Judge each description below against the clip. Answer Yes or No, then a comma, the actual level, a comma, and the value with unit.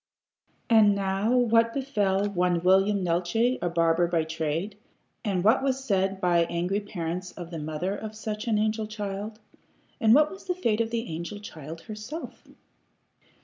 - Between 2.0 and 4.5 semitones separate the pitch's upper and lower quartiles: Yes, average, 4.1 semitones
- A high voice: Yes, high, 200 Hz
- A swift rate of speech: No, average, 160 wpm